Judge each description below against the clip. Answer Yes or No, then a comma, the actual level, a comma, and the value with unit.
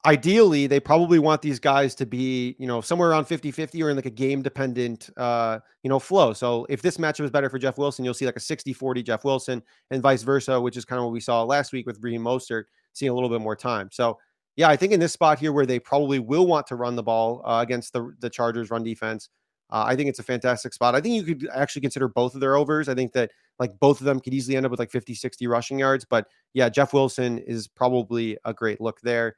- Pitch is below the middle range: Yes, low, 130 Hz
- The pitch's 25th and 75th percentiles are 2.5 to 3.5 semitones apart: Yes, average, 2.8 semitones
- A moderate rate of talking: No, fast, 265 wpm